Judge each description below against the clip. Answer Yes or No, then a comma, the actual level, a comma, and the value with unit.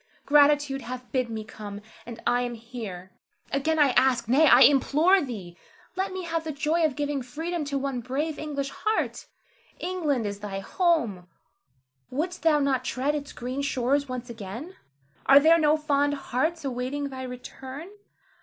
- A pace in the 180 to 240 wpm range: No, average, 165 wpm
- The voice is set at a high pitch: Yes, very high, 275 Hz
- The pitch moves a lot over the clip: No, average, 3.8 semitones